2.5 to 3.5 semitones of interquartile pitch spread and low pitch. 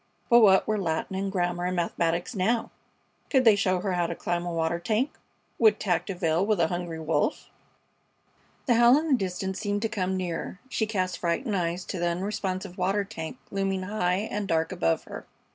No: average, 3.1 semitones; medium, 185 Hz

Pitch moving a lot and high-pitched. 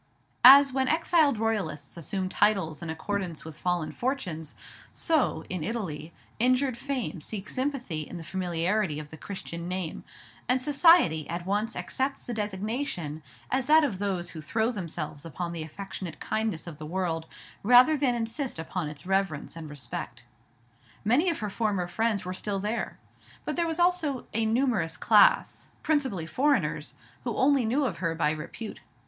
Yes: wide, 7.4 semitones; high, 200 Hz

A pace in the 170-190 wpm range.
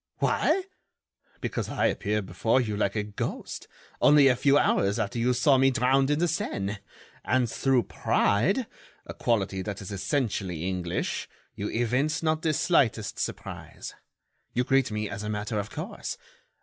No: average, 150 wpm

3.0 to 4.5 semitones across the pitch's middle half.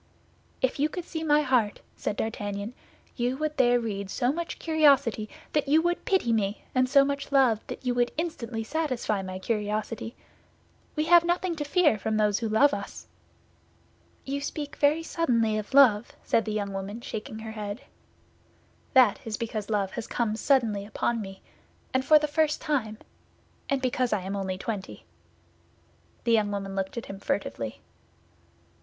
No: average, 5.3 semitones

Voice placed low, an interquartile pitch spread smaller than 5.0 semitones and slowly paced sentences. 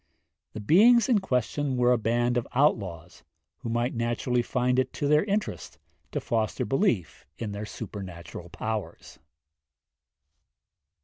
Yes: low, 120 Hz; average, 4.1 semitones; slow, 130 wpm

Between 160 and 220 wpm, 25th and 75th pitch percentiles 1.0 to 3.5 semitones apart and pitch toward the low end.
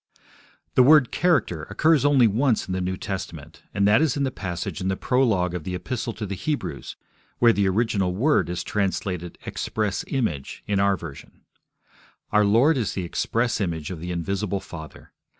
No: average, 180 wpm; average, 5.3 semitones; low, 100 Hz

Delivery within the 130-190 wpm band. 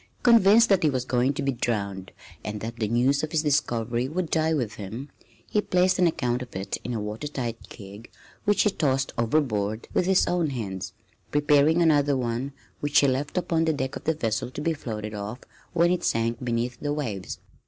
No: fast, 205 wpm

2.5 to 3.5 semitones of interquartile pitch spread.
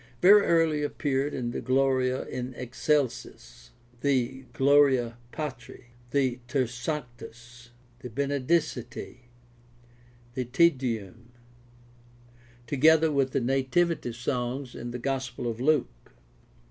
Yes: average, 2.8 semitones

